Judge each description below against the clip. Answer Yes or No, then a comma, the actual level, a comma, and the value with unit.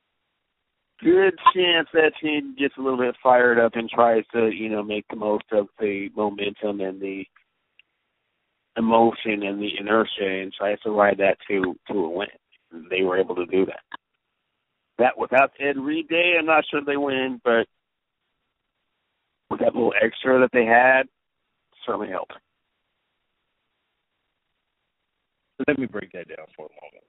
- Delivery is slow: No, average, 160 wpm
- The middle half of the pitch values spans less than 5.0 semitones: No, average, 5.3 semitones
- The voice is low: Yes, low, 115 Hz